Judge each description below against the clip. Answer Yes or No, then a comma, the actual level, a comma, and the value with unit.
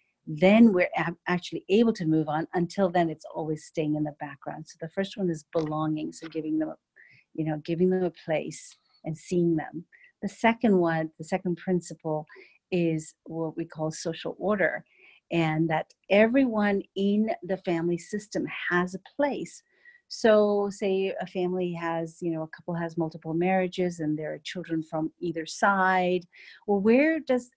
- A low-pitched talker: No, medium, 175 Hz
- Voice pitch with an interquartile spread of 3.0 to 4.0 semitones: Yes, average, 3.6 semitones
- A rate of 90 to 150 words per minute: No, average, 170 wpm